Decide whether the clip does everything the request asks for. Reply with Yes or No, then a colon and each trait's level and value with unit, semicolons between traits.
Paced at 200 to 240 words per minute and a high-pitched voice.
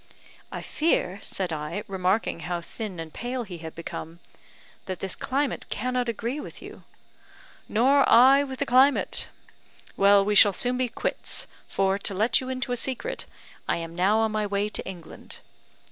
No: average, 170 wpm; high, 210 Hz